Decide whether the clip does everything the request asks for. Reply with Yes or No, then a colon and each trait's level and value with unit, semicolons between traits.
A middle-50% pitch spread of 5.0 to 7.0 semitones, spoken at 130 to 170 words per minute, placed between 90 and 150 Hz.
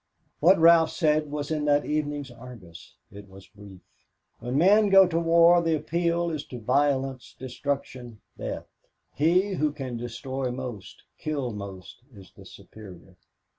Yes: average, 5.3 semitones; average, 145 wpm; medium, 140 Hz